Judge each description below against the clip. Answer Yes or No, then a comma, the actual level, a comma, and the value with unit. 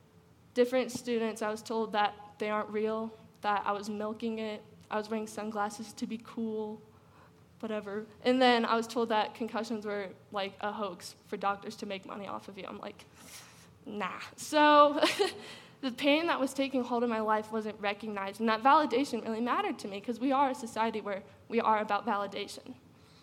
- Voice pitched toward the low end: No, high, 220 Hz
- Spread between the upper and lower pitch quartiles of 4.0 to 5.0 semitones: No, narrow, 2.4 semitones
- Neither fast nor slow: Yes, average, 190 wpm